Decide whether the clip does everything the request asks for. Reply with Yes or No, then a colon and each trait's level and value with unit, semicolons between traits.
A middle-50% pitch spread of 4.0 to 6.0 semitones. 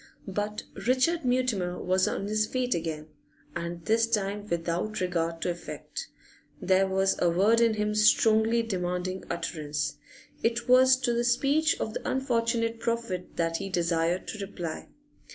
Yes: average, 4.6 semitones